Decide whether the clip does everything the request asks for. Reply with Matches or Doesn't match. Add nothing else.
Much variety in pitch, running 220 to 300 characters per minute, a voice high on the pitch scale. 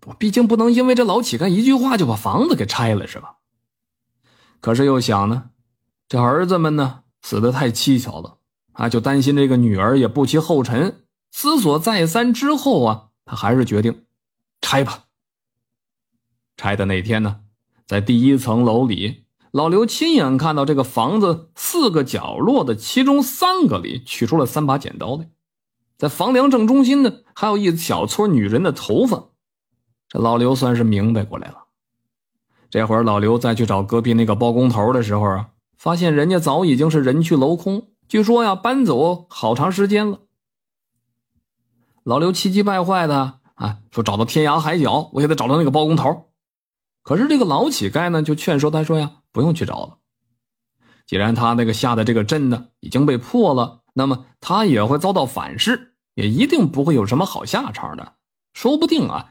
Doesn't match